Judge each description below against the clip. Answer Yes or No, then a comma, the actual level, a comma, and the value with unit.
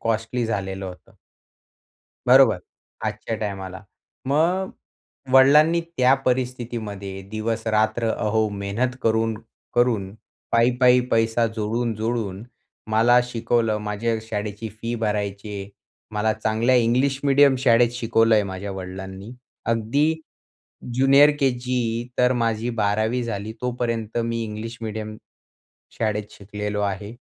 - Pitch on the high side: No, low, 115 Hz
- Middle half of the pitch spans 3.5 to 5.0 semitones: No, average, 2.7 semitones